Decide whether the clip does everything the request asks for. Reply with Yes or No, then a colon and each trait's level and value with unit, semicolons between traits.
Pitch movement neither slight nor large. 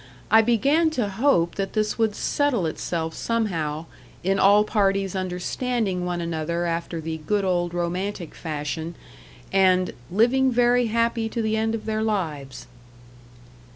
Yes: average, 4.6 semitones